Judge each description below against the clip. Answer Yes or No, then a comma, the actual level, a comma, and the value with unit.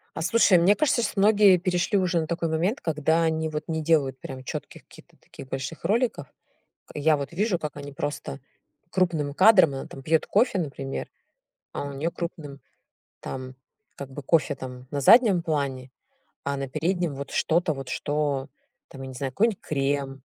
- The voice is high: No, medium, 155 Hz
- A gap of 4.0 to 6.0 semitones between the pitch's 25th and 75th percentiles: Yes, average, 4.3 semitones